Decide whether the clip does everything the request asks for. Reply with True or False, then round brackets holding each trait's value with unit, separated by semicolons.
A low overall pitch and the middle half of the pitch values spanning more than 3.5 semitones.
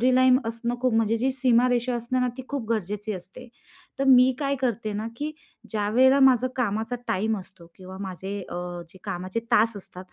False (230 Hz; 3.9 semitones)